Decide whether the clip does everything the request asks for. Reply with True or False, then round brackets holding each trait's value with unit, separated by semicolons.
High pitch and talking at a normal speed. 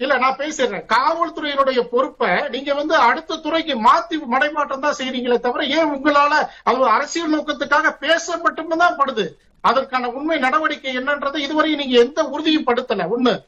False (290 Hz; 140 wpm)